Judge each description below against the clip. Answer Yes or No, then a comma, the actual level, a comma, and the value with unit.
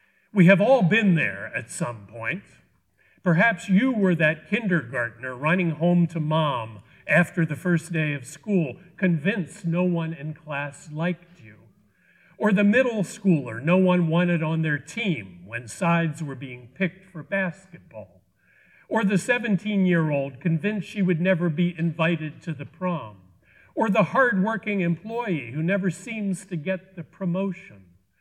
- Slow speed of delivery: No, average, 150 wpm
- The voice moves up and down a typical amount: Yes, average, 3.7 semitones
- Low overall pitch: No, medium, 175 Hz